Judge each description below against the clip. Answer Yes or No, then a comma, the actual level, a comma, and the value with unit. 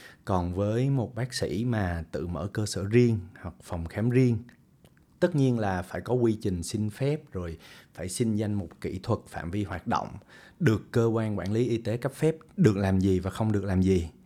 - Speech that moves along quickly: No, average, 220 wpm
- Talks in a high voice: No, low, 105 Hz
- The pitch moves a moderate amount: Yes, average, 4.6 semitones